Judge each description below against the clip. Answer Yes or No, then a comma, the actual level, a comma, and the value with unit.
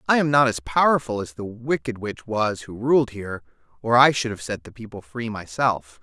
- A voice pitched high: No, low, 115 Hz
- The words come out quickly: Yes, fast, 220 wpm